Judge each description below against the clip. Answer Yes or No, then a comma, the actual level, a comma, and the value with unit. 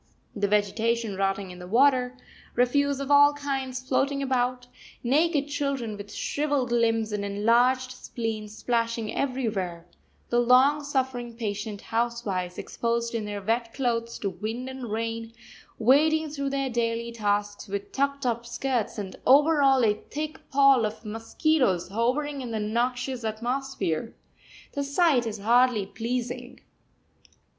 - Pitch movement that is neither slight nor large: Yes, average, 3.6 semitones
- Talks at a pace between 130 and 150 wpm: Yes, slow, 135 wpm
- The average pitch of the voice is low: No, high, 240 Hz